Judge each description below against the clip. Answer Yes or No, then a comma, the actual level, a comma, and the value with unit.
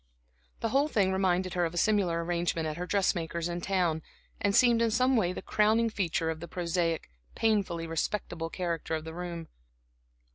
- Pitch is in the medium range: Yes, medium, 175 Hz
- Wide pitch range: No, average, 3.5 semitones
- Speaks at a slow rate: No, average, 180 wpm